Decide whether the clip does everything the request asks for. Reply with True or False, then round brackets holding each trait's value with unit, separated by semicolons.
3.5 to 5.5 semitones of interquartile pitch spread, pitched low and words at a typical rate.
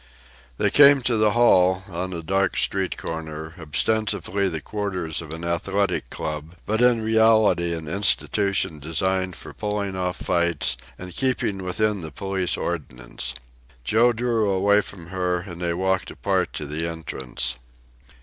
True (4.0 semitones; 95 Hz; 150 wpm)